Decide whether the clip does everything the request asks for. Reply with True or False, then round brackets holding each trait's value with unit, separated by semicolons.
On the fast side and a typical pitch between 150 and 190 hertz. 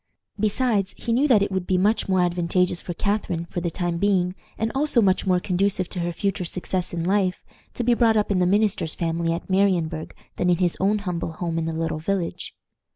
True (220 wpm; 185 Hz)